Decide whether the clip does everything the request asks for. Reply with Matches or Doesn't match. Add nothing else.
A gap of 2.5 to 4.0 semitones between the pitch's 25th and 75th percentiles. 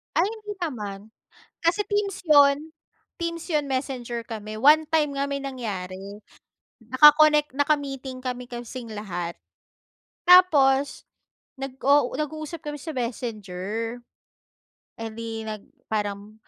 Doesn't match